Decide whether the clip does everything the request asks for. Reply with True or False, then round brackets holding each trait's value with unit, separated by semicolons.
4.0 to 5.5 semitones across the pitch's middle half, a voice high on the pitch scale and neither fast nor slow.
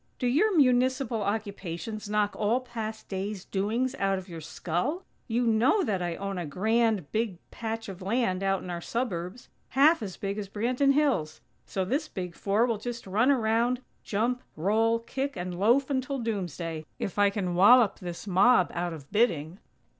True (4.6 semitones; 215 Hz; 175 wpm)